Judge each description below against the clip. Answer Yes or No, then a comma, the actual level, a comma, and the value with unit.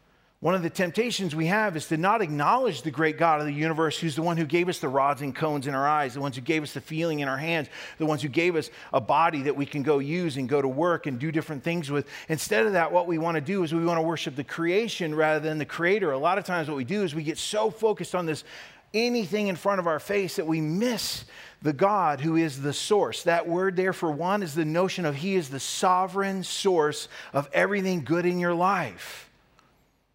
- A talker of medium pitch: Yes, medium, 165 Hz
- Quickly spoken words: Yes, fast, 255 wpm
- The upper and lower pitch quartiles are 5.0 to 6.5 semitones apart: No, average, 3.3 semitones